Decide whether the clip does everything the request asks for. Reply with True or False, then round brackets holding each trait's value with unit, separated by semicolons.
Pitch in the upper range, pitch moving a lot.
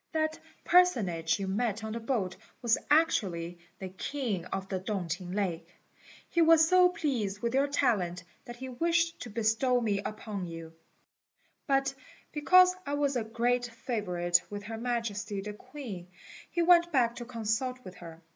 True (230 Hz; 6.0 semitones)